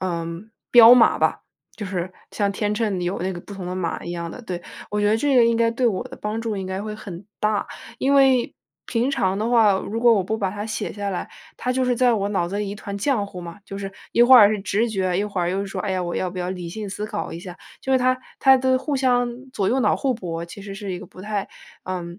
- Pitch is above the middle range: Yes, high, 205 Hz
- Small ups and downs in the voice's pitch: No, average, 3.8 semitones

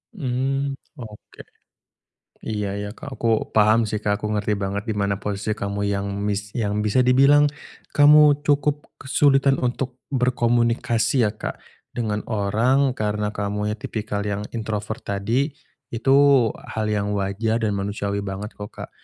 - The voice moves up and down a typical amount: Yes, average, 3.7 semitones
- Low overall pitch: Yes, low, 110 Hz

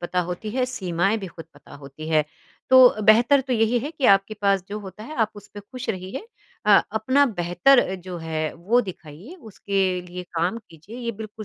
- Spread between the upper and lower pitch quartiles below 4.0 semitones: No, average, 4.8 semitones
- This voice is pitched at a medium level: No, high, 200 Hz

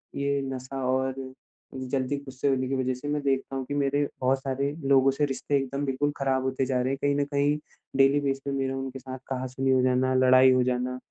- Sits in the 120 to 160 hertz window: Yes, low, 135 Hz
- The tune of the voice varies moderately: No, narrow, 1.1 semitones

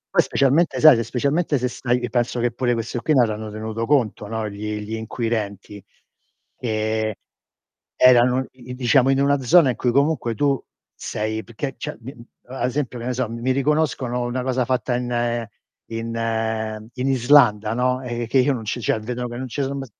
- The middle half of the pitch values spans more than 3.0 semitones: No, narrow, 2.6 semitones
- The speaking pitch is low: Yes, low, 120 Hz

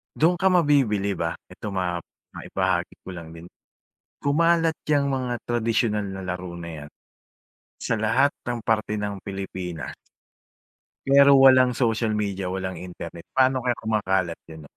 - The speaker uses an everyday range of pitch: No, wide, 6.1 semitones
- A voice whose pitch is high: No, low, 105 Hz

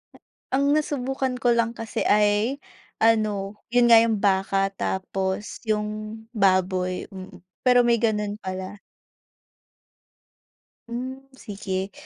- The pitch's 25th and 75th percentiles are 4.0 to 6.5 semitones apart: No, average, 3.5 semitones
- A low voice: No, high, 215 Hz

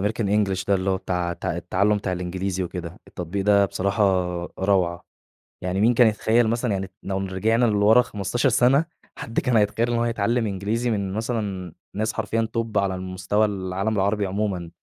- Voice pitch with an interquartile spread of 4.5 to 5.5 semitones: No, average, 3.0 semitones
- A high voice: No, low, 100 Hz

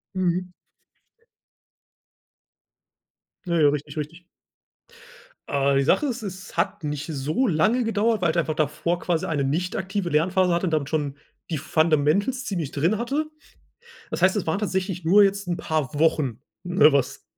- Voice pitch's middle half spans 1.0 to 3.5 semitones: No, average, 4.1 semitones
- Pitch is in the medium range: Yes, medium, 170 Hz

